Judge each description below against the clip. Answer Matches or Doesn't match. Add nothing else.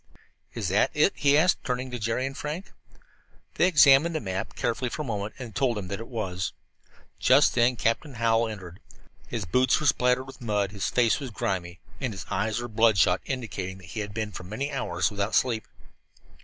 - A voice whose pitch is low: Matches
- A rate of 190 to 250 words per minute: Matches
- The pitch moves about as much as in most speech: Matches